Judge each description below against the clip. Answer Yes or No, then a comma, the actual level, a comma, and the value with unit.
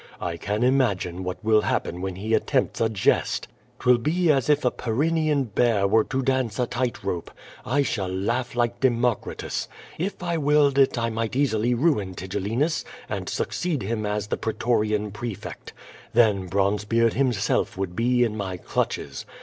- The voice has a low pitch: Yes, low, 115 Hz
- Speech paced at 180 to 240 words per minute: No, average, 165 wpm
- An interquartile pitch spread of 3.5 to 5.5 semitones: Yes, average, 4.2 semitones